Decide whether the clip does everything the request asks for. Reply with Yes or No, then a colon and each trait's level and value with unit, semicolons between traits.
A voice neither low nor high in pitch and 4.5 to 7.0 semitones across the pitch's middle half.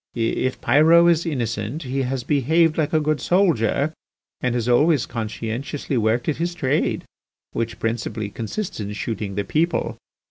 No: low, 130 Hz; wide, 5.6 semitones